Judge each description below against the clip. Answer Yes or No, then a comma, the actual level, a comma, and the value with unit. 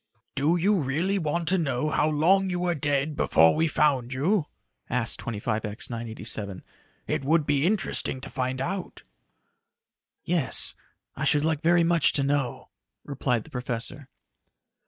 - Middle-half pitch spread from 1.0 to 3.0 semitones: No, average, 4.8 semitones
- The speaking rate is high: No, average, 145 wpm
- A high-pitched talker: No, medium, 145 Hz